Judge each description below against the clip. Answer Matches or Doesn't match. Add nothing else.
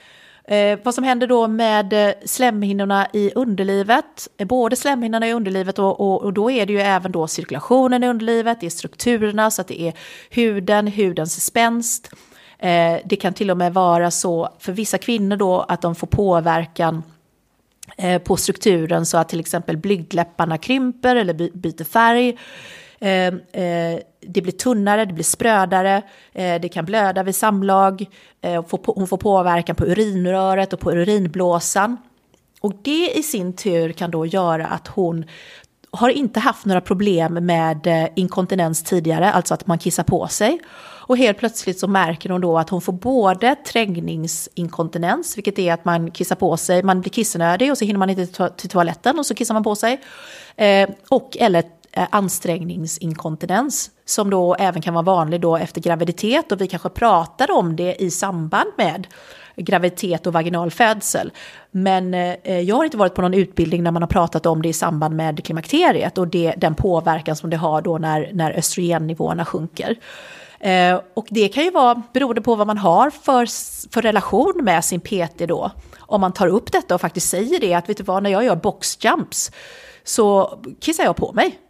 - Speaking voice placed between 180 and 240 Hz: Matches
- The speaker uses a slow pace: Doesn't match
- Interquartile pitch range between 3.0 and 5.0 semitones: Matches